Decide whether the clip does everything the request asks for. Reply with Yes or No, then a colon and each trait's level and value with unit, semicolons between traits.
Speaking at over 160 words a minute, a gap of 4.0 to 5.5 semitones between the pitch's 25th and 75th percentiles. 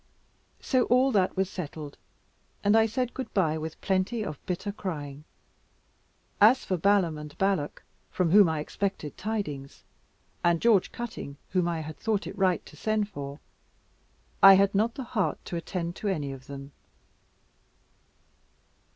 No: average, 150 wpm; average, 5.1 semitones